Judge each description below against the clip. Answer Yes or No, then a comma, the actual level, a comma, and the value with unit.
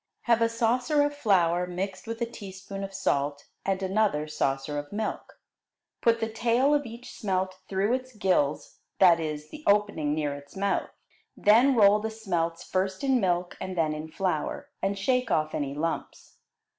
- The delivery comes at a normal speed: Yes, average, 170 wpm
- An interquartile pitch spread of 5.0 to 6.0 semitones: Yes, wide, 5.6 semitones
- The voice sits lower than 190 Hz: No, high, 195 Hz